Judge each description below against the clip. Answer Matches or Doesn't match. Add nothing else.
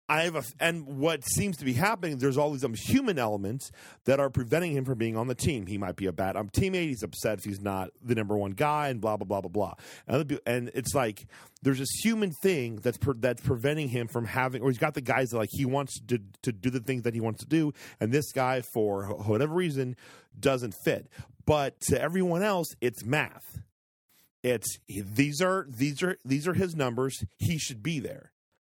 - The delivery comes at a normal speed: Doesn't match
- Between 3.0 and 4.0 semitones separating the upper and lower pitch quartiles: Doesn't match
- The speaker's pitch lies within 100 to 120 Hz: Doesn't match